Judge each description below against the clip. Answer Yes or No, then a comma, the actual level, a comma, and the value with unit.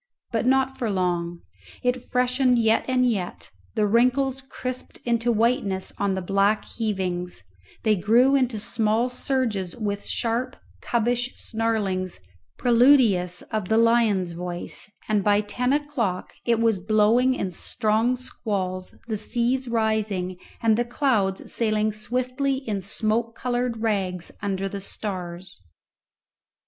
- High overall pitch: Yes, high, 220 Hz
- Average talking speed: No, slow, 130 wpm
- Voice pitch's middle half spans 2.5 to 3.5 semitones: No, average, 4.1 semitones